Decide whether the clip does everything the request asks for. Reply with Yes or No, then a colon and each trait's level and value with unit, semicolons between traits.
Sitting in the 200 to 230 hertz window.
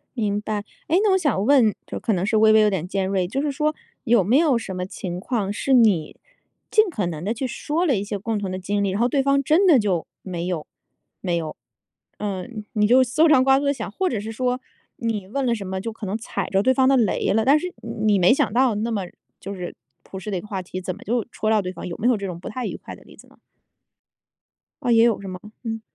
Yes: high, 215 Hz